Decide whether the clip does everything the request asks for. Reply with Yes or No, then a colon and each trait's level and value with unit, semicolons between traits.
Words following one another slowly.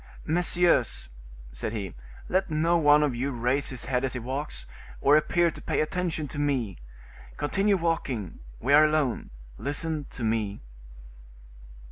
No: average, 145 wpm